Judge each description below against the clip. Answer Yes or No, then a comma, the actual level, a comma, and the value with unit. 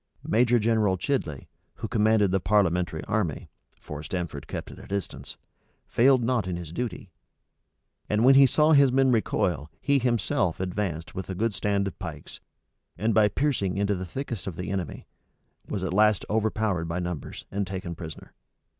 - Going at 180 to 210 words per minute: No, average, 165 wpm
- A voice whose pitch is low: Yes, low, 100 Hz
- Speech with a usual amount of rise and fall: Yes, average, 4.3 semitones